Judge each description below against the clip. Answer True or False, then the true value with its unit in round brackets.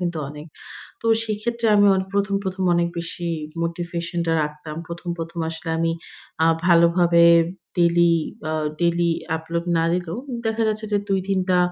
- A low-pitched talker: False (170 Hz)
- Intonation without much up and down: True (2.1 semitones)